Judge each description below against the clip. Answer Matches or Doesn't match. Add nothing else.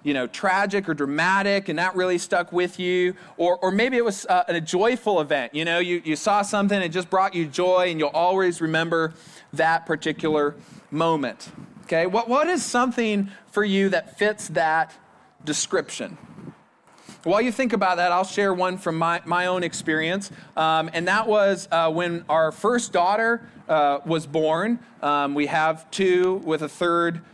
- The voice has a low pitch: Doesn't match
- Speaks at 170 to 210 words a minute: Matches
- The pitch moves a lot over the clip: Doesn't match